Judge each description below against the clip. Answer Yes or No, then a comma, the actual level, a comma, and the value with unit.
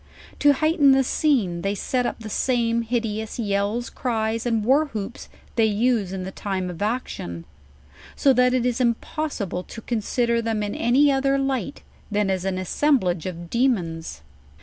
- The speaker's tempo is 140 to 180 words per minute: Yes, average, 165 wpm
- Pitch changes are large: No, average, 4.4 semitones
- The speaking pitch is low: No, high, 230 Hz